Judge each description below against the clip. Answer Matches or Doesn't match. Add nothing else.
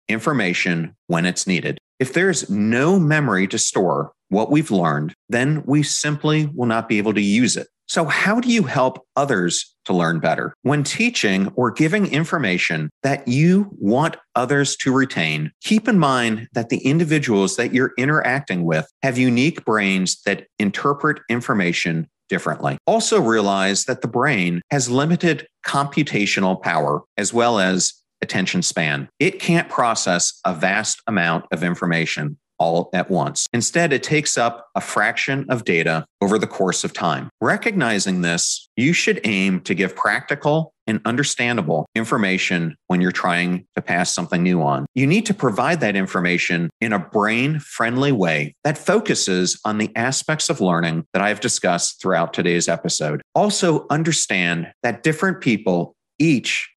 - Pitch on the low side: Matches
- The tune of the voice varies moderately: Doesn't match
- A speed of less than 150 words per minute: Doesn't match